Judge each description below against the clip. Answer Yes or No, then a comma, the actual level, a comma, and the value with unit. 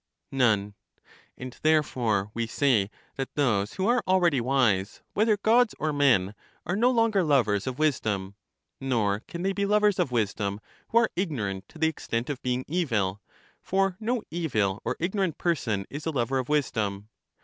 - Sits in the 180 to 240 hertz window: No, low, 135 Hz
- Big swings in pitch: Yes, wide, 8.8 semitones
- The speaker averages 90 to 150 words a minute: No, average, 165 wpm